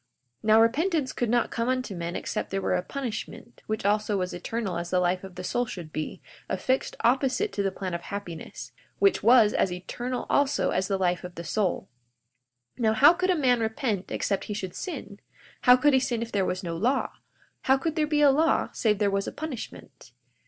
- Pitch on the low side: No, high, 220 Hz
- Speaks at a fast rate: Yes, fast, 215 wpm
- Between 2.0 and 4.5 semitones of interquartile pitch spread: No, wide, 5.6 semitones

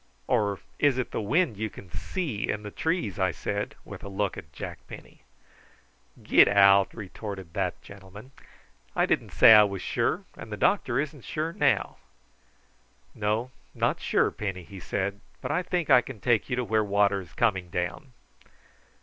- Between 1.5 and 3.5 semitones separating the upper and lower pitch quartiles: No, average, 4.3 semitones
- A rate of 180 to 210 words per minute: No, average, 170 wpm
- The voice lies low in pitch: Yes, low, 105 Hz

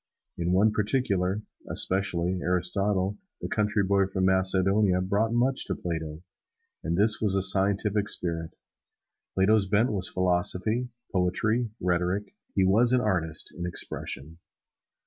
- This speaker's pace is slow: Yes, slow, 125 wpm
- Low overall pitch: Yes, very low, 95 Hz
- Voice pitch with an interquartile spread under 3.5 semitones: Yes, average, 2.8 semitones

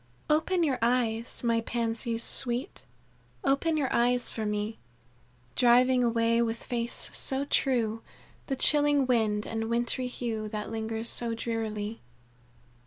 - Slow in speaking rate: Yes, slow, 125 wpm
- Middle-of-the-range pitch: No, high, 235 Hz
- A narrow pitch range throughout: Yes, narrow, 2.1 semitones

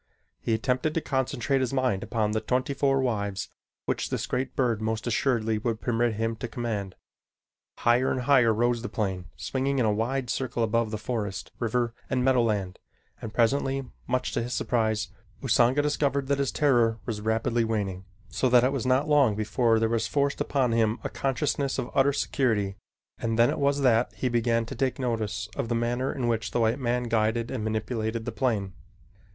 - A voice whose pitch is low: Yes, low, 120 Hz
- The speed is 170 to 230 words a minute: Yes, average, 190 wpm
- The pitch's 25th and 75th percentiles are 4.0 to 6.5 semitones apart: No, average, 2.8 semitones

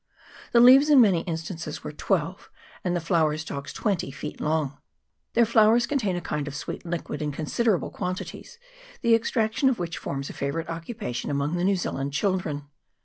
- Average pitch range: No, wide, 6.5 semitones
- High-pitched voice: No, medium, 170 Hz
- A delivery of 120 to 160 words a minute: No, average, 180 wpm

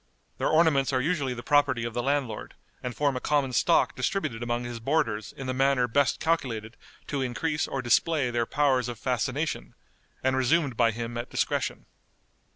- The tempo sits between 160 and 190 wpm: Yes, average, 175 wpm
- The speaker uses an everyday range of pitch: Yes, average, 3.3 semitones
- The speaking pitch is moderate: No, low, 130 Hz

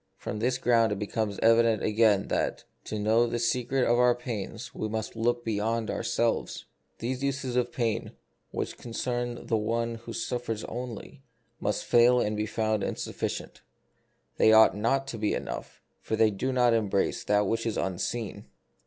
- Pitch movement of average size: No, narrow, 1.9 semitones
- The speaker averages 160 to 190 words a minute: Yes, average, 170 wpm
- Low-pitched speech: Yes, low, 115 Hz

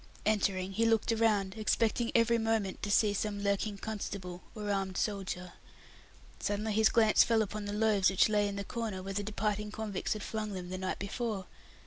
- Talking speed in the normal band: Yes, average, 190 wpm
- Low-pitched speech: No, high, 205 Hz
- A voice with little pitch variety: Yes, narrow, 2.0 semitones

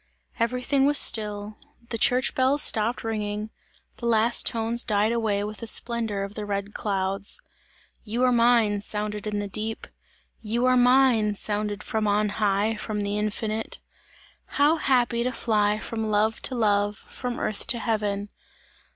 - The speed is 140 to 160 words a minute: Yes, average, 155 wpm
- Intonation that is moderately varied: No, narrow, 2.3 semitones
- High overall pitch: Yes, high, 215 Hz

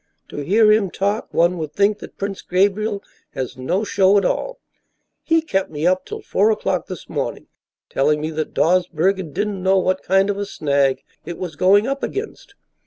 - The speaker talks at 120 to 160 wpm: No, average, 185 wpm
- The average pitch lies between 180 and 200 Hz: Yes, high, 190 Hz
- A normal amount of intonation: Yes, average, 3.8 semitones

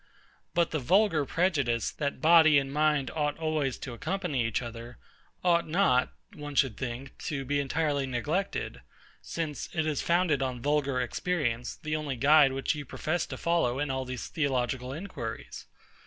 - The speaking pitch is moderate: Yes, medium, 145 Hz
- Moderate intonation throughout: Yes, average, 3.6 semitones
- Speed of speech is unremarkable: Yes, average, 160 wpm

